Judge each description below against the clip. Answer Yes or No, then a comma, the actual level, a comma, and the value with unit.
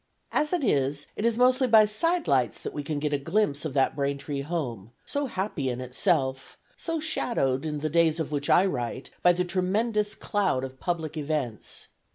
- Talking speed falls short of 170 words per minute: No, average, 195 wpm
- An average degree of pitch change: No, wide, 7.3 semitones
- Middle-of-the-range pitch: Yes, medium, 155 Hz